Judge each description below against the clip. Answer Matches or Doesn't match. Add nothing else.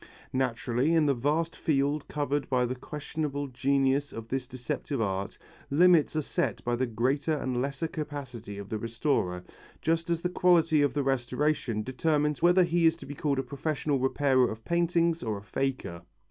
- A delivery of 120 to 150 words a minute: Doesn't match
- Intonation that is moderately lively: Matches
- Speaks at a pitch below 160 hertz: Matches